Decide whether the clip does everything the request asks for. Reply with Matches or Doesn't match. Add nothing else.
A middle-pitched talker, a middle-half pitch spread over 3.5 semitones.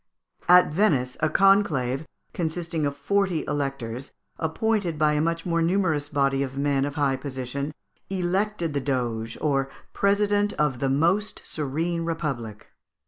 Matches